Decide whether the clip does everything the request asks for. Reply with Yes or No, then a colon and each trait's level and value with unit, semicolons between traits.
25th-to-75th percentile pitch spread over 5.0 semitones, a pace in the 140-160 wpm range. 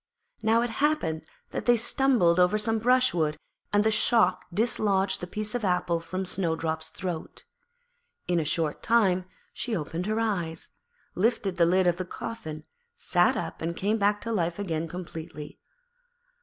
No: average, 4.7 semitones; average, 155 wpm